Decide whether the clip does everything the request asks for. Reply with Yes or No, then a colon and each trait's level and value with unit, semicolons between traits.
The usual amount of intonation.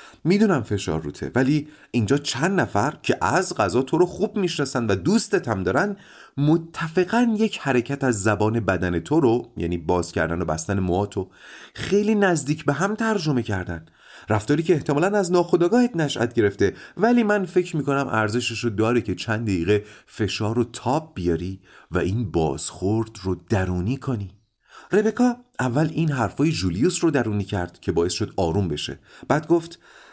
No: wide, 9.0 semitones